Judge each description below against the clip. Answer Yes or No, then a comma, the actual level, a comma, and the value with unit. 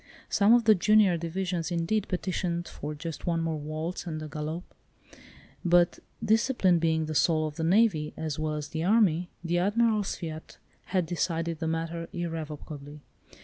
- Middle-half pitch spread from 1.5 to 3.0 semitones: Yes, narrow, 2.6 semitones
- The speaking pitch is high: No, medium, 170 Hz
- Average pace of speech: Yes, average, 160 wpm